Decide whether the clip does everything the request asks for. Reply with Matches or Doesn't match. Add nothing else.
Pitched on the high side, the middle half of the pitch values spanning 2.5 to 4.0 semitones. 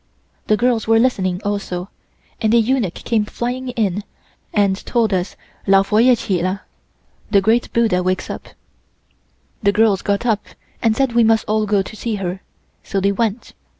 Matches